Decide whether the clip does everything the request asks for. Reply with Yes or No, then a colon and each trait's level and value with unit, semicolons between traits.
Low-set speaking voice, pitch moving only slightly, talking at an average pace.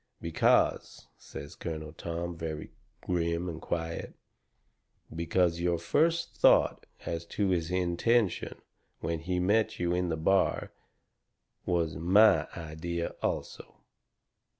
No: very low, 85 Hz; narrow, 1.7 semitones; slow, 110 wpm